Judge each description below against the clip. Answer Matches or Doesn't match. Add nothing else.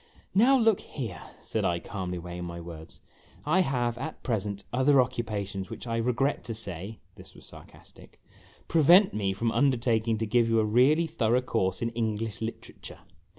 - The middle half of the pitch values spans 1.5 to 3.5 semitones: Doesn't match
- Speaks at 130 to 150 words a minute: Doesn't match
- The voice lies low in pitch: Matches